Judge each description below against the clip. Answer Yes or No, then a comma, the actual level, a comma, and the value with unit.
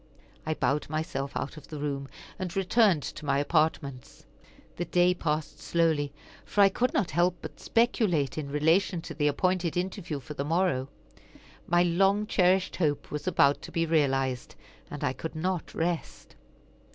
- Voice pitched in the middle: Yes, medium, 160 Hz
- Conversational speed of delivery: Yes, average, 165 wpm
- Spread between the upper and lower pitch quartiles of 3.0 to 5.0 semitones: Yes, average, 3.8 semitones